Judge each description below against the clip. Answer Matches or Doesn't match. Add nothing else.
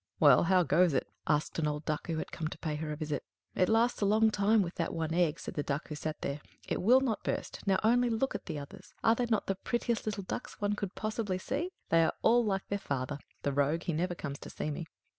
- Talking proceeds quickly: Matches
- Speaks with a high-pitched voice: Doesn't match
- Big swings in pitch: Matches